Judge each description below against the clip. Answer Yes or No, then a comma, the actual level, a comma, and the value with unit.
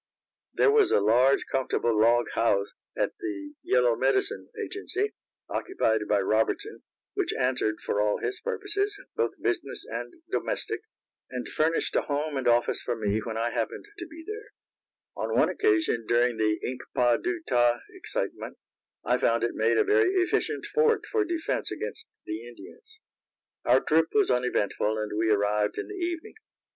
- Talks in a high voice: No, medium, 155 Hz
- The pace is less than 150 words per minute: No, average, 165 wpm